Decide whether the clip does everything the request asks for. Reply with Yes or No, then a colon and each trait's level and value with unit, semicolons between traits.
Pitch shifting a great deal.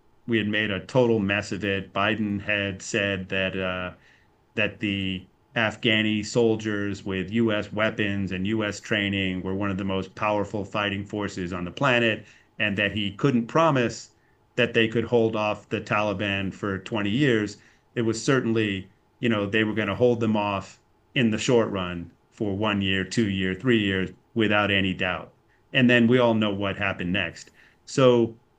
No: average, 2.7 semitones